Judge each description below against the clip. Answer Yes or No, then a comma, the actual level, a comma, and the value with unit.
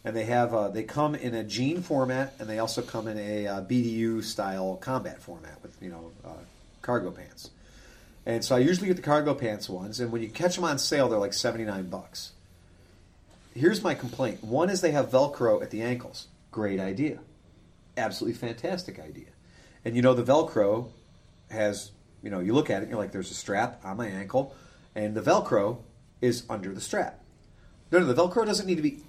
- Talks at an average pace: No, fast, 210 wpm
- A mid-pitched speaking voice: No, low, 115 Hz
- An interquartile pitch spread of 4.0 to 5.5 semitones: Yes, average, 4.7 semitones